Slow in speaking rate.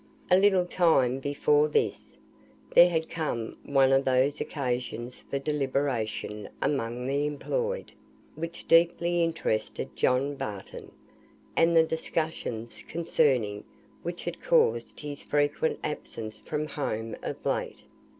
Yes: slow, 120 wpm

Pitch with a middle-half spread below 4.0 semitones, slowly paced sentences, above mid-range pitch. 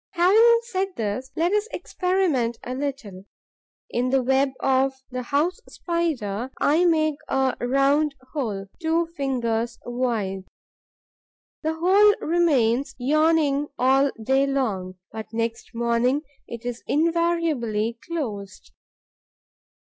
No: wide, 5.6 semitones; slow, 110 wpm; very high, 270 Hz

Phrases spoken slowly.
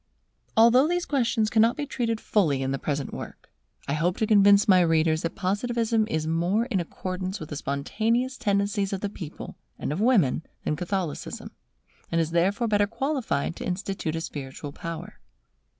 No: average, 170 wpm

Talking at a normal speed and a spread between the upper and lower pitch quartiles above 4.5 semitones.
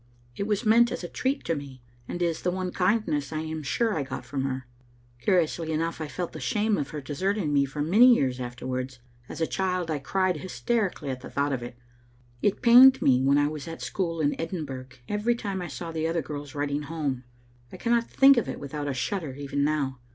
No: fast, 220 wpm; average, 5.2 semitones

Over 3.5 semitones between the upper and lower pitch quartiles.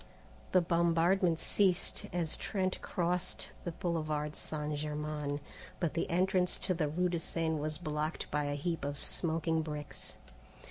No: narrow, 2.6 semitones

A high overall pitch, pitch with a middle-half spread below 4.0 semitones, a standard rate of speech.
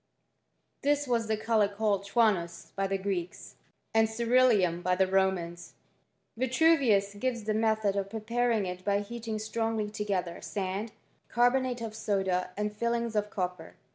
Yes: high, 210 Hz; average, 3.2 semitones; average, 160 wpm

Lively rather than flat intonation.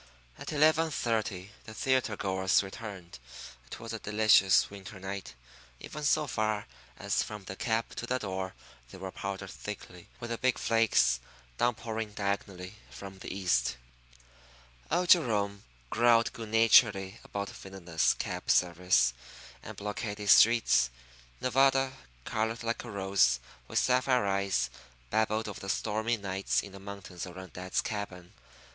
No: average, 3.2 semitones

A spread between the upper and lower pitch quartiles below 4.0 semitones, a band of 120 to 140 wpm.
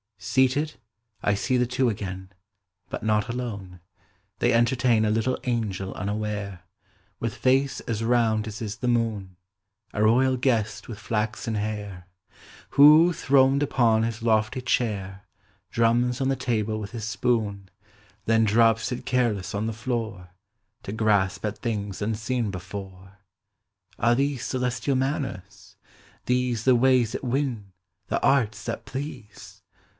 Yes: average, 3.5 semitones; slow, 135 wpm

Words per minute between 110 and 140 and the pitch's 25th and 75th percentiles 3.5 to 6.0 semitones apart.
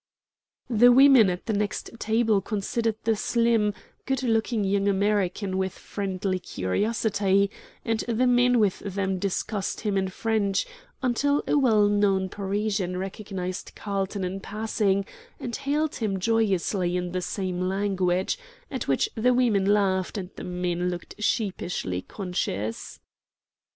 No: slow, 135 wpm; average, 2.9 semitones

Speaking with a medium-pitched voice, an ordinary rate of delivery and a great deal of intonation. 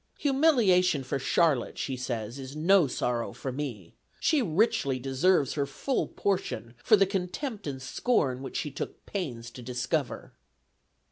Yes: medium, 145 Hz; average, 145 wpm; wide, 7.1 semitones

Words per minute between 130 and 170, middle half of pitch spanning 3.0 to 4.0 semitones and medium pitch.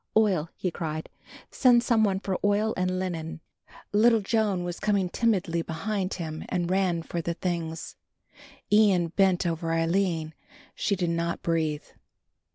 Yes: average, 140 wpm; average, 3.5 semitones; medium, 180 Hz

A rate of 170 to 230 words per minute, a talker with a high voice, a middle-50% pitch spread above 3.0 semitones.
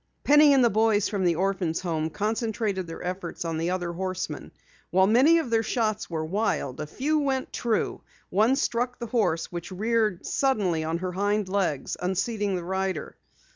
Yes: average, 175 wpm; high, 195 Hz; average, 4.5 semitones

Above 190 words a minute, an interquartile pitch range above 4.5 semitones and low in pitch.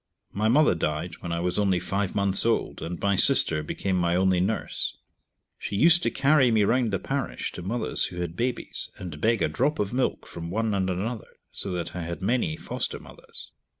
Yes: fast, 205 wpm; average, 4.9 semitones; low, 100 Hz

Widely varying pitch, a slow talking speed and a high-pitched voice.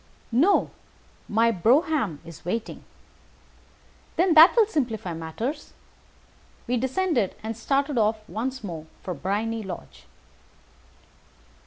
Yes: wide, 5.9 semitones; slow, 105 wpm; high, 230 Hz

